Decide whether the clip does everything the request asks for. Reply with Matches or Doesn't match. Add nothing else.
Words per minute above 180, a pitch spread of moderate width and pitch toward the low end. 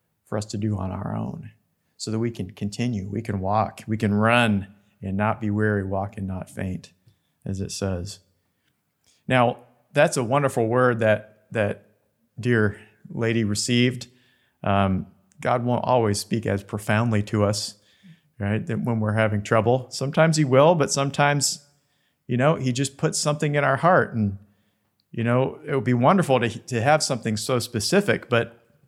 Doesn't match